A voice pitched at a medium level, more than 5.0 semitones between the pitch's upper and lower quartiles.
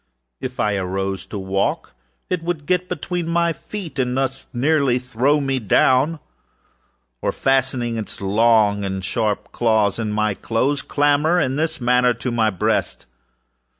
No: low, 125 Hz; wide, 5.4 semitones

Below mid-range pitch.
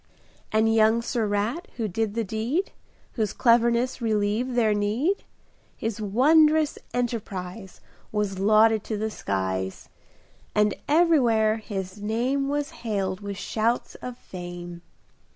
No: high, 220 Hz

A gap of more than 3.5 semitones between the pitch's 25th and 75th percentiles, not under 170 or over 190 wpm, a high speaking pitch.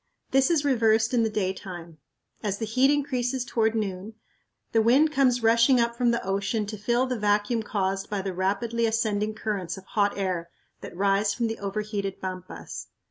No: average, 3.1 semitones; average, 180 wpm; high, 215 Hz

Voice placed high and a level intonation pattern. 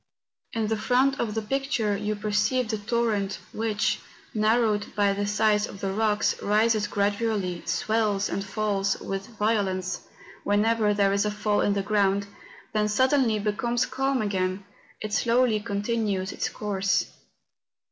Yes: high, 210 Hz; narrow, 1.9 semitones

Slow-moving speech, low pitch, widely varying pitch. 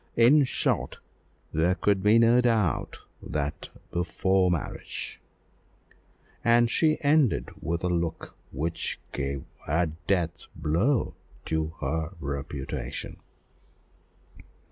Yes: slow, 100 wpm; very low, 85 Hz; wide, 6.8 semitones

